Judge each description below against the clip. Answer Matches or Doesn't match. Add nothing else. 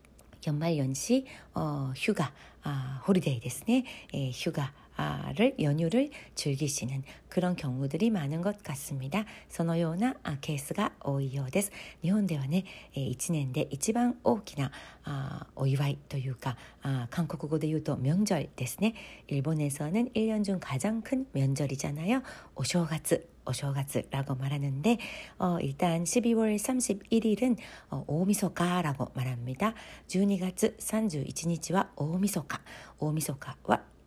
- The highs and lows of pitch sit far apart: Matches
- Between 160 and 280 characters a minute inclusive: Matches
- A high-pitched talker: Doesn't match